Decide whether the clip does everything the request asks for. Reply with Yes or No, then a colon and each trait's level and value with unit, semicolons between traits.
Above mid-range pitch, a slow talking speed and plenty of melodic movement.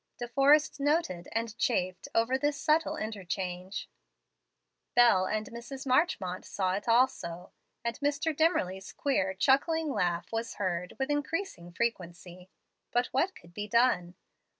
Yes: high, 230 Hz; slow, 130 wpm; wide, 7.2 semitones